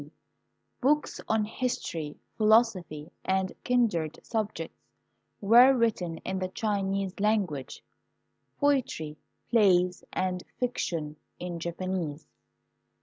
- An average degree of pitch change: Yes, average, 4.8 semitones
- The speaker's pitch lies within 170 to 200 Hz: Yes, high, 190 Hz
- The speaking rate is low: Yes, slow, 90 wpm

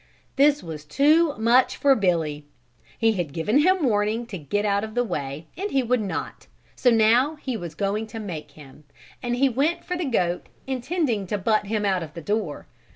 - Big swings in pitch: Yes, wide, 6.7 semitones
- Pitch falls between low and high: No, high, 220 Hz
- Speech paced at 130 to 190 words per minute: No, average, 200 wpm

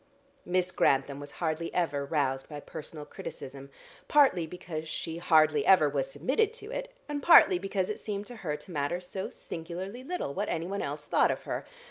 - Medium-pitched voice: Yes, medium, 170 Hz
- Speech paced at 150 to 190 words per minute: Yes, average, 180 wpm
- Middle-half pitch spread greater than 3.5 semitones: Yes, average, 5.1 semitones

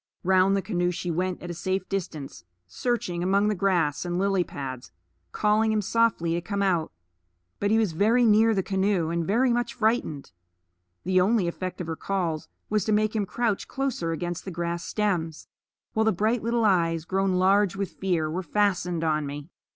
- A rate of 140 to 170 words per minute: No, average, 190 wpm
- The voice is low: No, high, 190 Hz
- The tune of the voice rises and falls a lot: No, average, 3.6 semitones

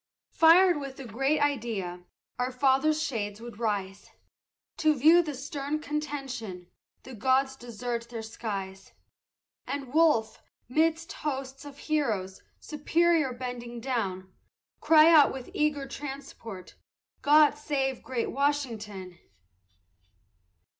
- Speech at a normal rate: No, slow, 110 wpm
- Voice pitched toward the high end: Yes, very high, 265 Hz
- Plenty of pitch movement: No, average, 4.6 semitones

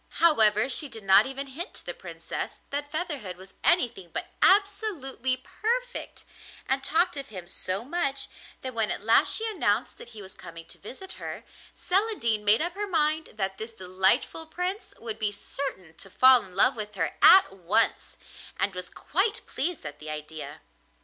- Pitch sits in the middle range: No, very high, 260 Hz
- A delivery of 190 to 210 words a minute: No, average, 175 wpm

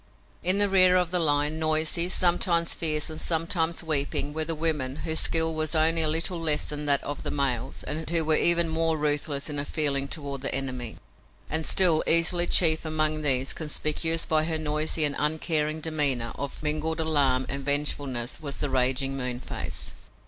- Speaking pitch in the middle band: Yes, medium, 155 Hz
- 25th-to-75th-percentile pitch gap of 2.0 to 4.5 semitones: Yes, narrow, 2.4 semitones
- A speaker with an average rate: Yes, average, 180 wpm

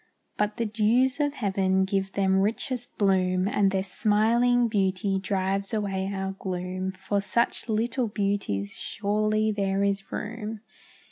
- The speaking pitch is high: Yes, high, 200 Hz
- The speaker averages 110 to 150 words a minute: Yes, slow, 135 wpm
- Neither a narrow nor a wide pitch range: No, narrow, 2.2 semitones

